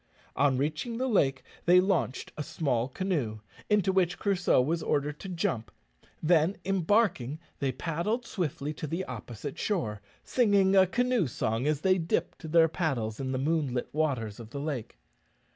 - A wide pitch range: Yes, wide, 6.2 semitones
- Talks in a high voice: No, medium, 155 Hz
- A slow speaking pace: No, average, 160 wpm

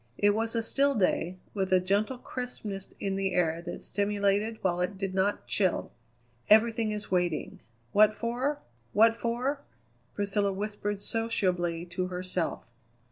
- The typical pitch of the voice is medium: No, high, 205 Hz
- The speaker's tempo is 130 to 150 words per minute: Yes, average, 140 wpm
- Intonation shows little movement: No, average, 3.4 semitones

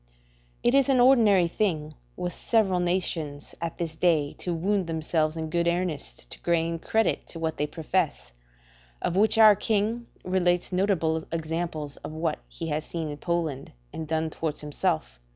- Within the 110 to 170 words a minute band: Yes, average, 165 wpm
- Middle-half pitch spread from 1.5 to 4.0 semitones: Yes, average, 3.1 semitones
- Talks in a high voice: No, medium, 170 Hz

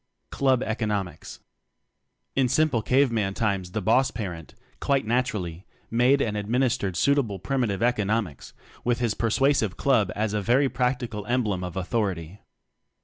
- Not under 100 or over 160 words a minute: Yes, average, 145 wpm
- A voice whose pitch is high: No, low, 115 Hz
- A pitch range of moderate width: Yes, average, 4.2 semitones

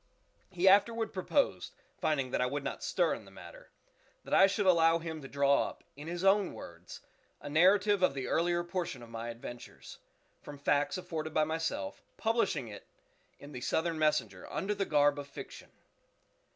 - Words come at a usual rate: Yes, average, 180 wpm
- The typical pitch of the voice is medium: Yes, medium, 160 Hz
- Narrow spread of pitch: No, average, 4.9 semitones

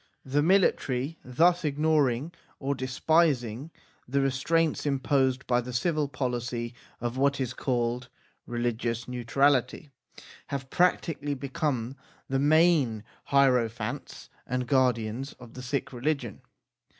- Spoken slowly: Yes, slow, 115 wpm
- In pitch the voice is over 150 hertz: No, low, 130 Hz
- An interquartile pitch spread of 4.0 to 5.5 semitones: No, average, 3.0 semitones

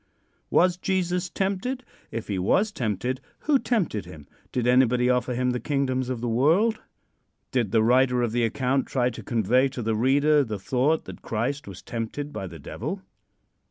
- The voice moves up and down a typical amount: Yes, average, 4.3 semitones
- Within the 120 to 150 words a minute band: No, average, 175 wpm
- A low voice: Yes, low, 125 Hz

